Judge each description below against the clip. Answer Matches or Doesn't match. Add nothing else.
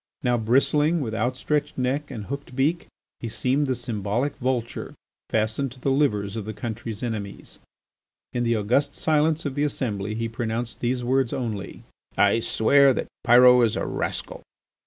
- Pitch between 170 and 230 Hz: Doesn't match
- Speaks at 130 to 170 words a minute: Matches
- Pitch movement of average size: Matches